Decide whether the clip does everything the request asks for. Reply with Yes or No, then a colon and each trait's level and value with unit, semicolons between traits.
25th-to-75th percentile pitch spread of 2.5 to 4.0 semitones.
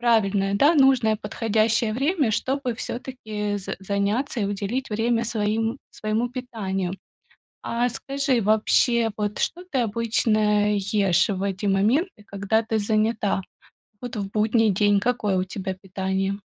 Yes: average, 2.9 semitones